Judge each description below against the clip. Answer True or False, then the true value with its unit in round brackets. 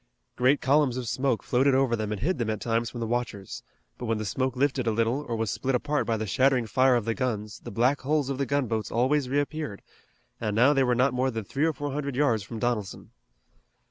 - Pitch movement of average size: True (3.4 semitones)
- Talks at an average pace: False (235 wpm)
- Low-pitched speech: True (125 Hz)